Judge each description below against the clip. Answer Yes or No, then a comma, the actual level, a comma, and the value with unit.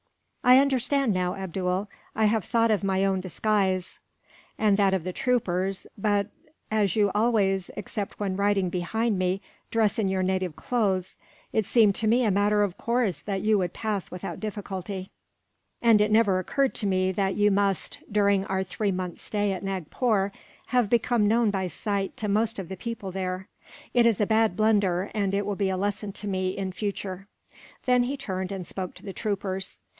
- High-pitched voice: Yes, high, 200 Hz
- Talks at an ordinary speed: Yes, average, 190 wpm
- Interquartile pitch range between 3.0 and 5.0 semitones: No, narrow, 2.5 semitones